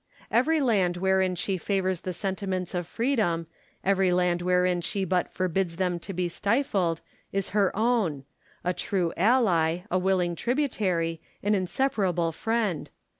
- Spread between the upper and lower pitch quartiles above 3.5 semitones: No, average, 2.7 semitones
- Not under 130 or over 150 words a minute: Yes, average, 140 wpm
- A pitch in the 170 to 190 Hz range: Yes, medium, 185 Hz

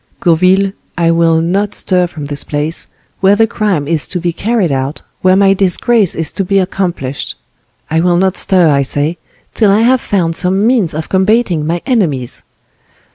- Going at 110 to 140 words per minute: No, average, 180 wpm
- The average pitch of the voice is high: No, medium, 180 Hz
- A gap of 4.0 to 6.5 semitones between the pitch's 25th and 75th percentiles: No, average, 3.5 semitones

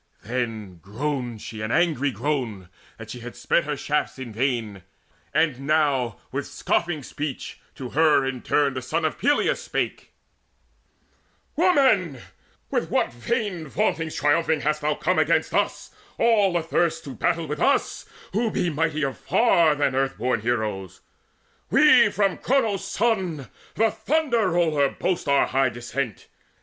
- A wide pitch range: Yes, wide, 5.7 semitones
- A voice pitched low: No, medium, 150 Hz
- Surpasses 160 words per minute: No, average, 145 wpm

